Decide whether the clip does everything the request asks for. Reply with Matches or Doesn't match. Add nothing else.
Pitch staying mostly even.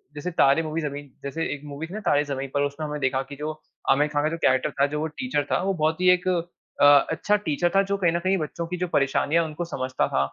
Doesn't match